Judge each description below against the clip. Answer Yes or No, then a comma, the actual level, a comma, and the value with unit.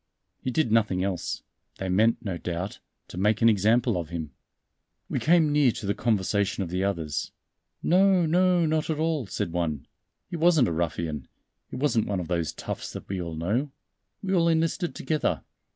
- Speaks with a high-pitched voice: No, low, 105 Hz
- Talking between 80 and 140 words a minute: No, average, 185 wpm